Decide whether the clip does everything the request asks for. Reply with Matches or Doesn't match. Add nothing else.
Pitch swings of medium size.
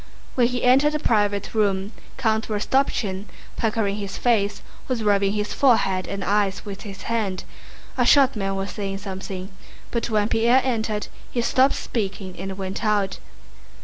Matches